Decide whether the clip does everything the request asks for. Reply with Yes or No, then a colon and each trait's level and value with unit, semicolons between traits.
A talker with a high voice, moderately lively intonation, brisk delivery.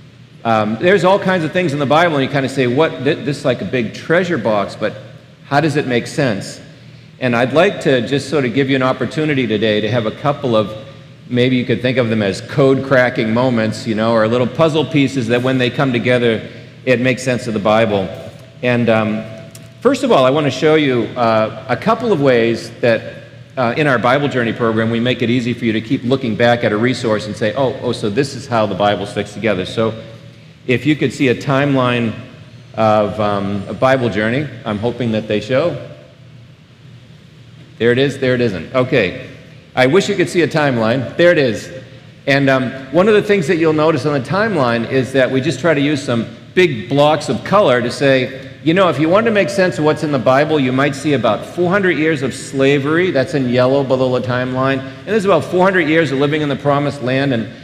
No: low, 130 Hz; average, 3.6 semitones; fast, 230 wpm